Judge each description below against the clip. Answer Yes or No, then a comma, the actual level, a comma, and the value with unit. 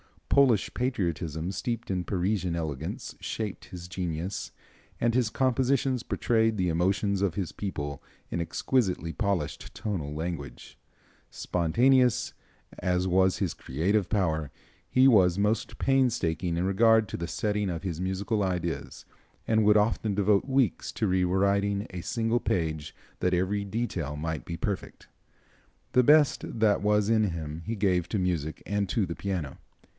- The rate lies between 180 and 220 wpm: No, average, 145 wpm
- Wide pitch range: No, average, 4.2 semitones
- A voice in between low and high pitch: No, very low, 95 Hz